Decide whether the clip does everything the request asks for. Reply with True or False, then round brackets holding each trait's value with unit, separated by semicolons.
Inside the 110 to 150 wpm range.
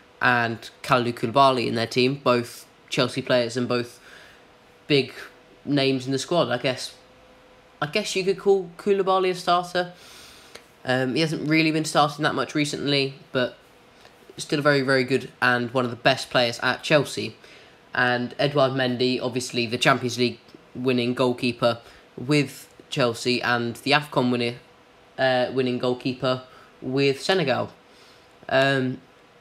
True (145 wpm)